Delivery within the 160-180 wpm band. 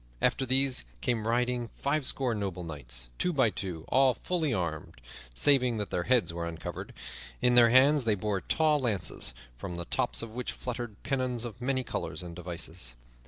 Yes: average, 170 wpm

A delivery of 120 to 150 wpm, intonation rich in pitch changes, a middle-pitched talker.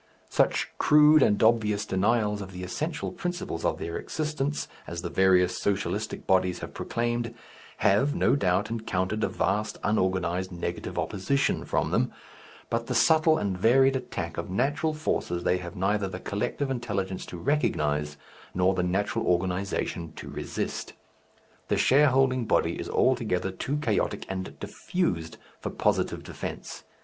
No: average, 145 wpm; wide, 6.0 semitones; low, 105 Hz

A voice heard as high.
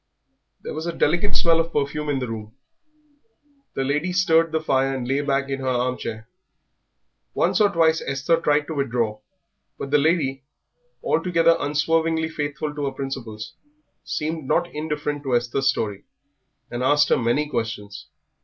No: medium, 145 Hz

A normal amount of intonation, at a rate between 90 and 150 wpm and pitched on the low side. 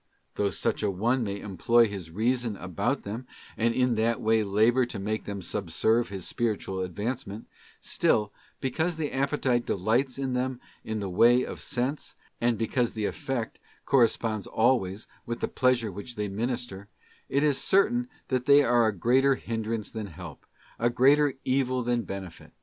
No: average, 3.8 semitones; average, 160 wpm; low, 115 Hz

